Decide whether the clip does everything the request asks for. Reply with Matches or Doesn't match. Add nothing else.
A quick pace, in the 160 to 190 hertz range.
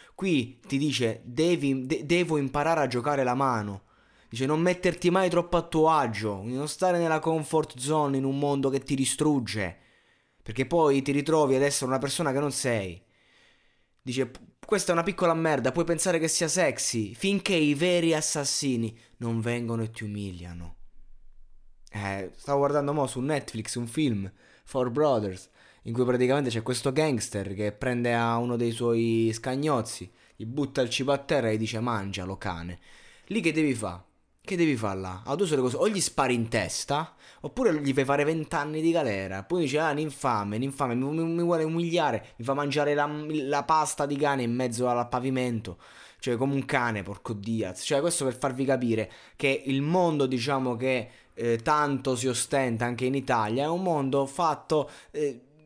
Doesn't match